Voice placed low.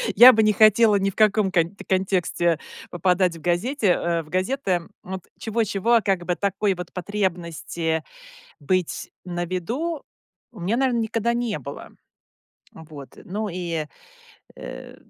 No: high, 190 Hz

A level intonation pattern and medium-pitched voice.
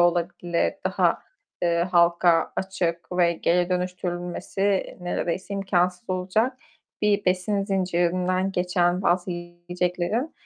Yes: narrow, 1.4 semitones; medium, 180 Hz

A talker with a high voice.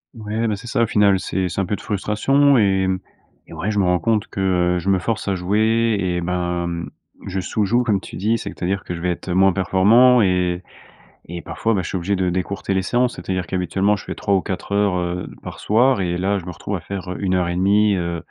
No: very low, 95 Hz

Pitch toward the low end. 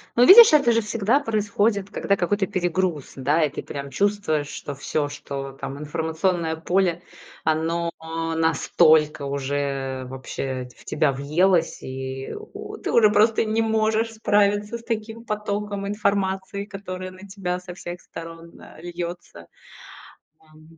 No: medium, 180 Hz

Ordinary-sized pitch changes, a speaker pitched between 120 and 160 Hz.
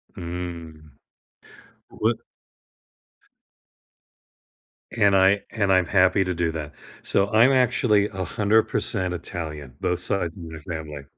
No: average, 3.6 semitones; very low, 90 Hz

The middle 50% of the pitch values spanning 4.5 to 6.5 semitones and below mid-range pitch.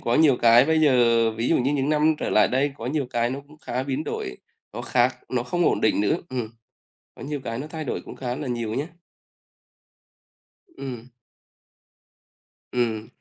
No: average, 3.6 semitones; low, 130 Hz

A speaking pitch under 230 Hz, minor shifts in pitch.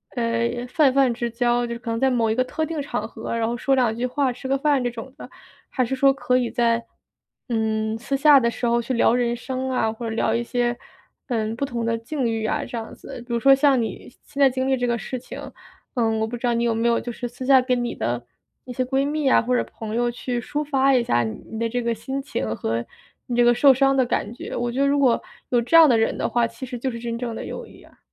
No: high, 240 Hz; narrow, 2.3 semitones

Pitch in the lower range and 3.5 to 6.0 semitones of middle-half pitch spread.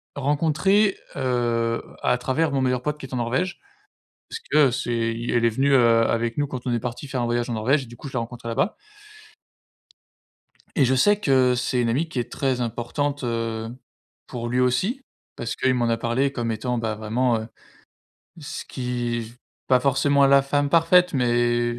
No: low, 125 Hz; average, 2.9 semitones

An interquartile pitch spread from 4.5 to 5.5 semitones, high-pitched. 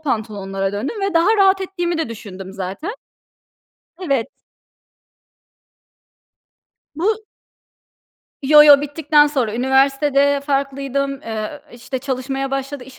No: average, 3.7 semitones; very high, 275 Hz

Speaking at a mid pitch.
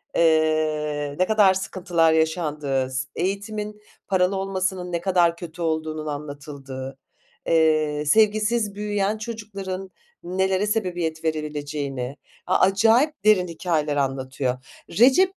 Yes: medium, 170 Hz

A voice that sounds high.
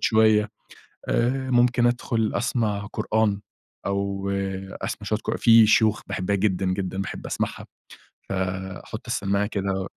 No: low, 105 Hz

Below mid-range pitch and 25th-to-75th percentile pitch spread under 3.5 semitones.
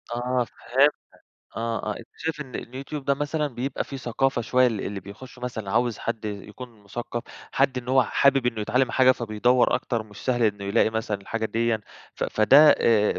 Yes: low, 120 Hz; average, 3.1 semitones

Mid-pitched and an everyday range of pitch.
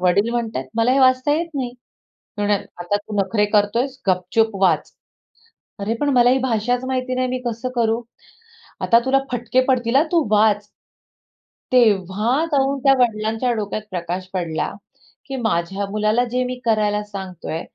No: high, 225 Hz; average, 3.7 semitones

